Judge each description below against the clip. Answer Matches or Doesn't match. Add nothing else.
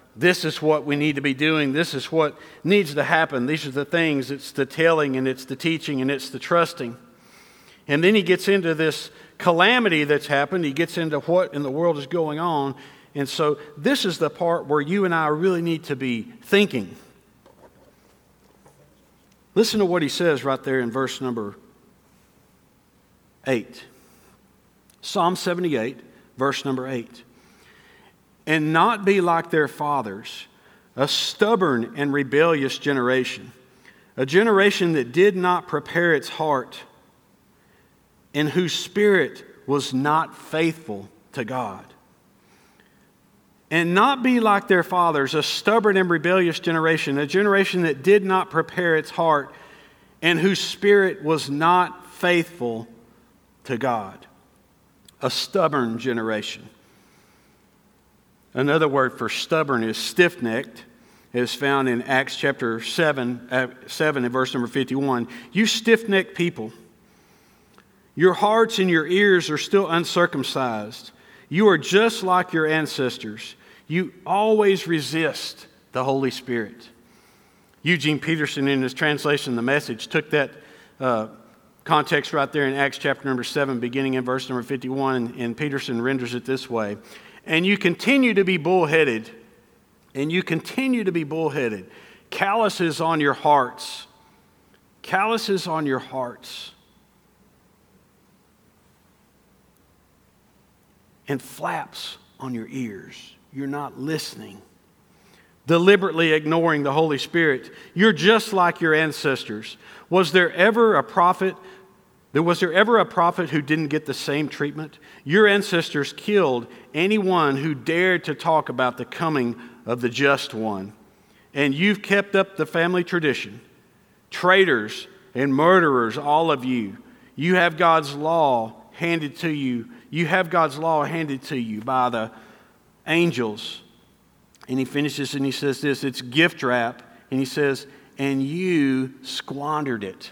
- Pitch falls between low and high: Matches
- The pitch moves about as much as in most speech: Matches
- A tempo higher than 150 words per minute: Doesn't match